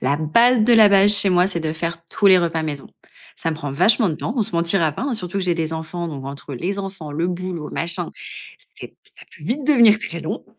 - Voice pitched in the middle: Yes, medium, 175 Hz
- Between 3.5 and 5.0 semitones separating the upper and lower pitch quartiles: Yes, average, 4.1 semitones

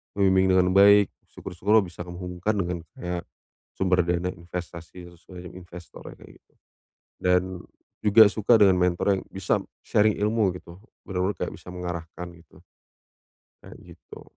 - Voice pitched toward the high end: No, very low, 90 Hz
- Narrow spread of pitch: Yes, narrow, 2.1 semitones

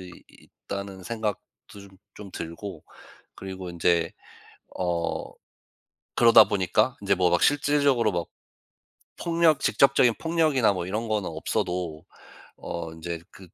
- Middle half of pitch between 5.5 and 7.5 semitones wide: No, average, 5.1 semitones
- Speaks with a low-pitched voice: Yes, low, 100 Hz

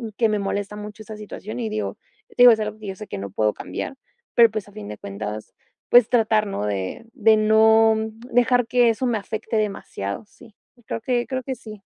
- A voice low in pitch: No, high, 215 Hz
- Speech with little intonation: Yes, narrow, 2.1 semitones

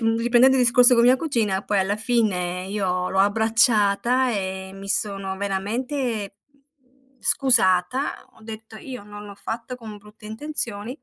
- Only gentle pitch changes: No, average, 3.8 semitones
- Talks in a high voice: Yes, high, 220 Hz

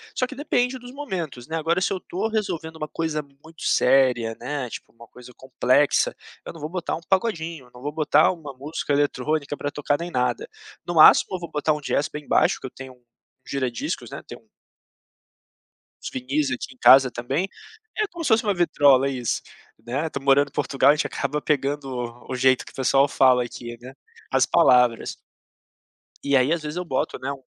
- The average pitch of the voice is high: No, medium, 145 Hz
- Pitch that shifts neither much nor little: Yes, average, 4.0 semitones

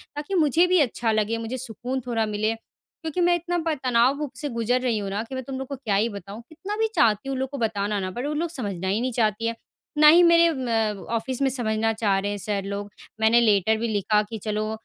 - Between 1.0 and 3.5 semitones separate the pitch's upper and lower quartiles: No, average, 4.5 semitones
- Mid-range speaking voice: No, high, 230 Hz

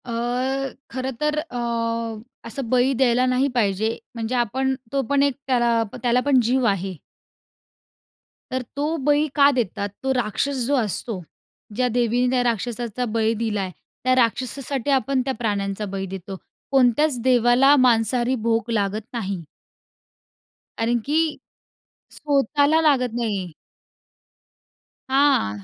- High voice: Yes, high, 245 Hz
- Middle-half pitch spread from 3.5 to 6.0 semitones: No, average, 3.0 semitones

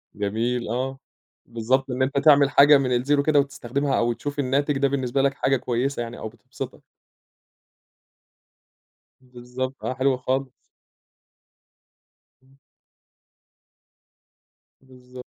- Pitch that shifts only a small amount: Yes, narrow, 2.0 semitones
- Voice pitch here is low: Yes, low, 130 Hz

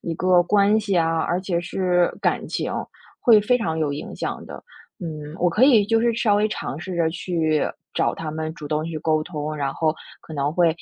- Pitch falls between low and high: Yes, medium, 170 Hz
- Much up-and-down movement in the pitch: No, average, 4.2 semitones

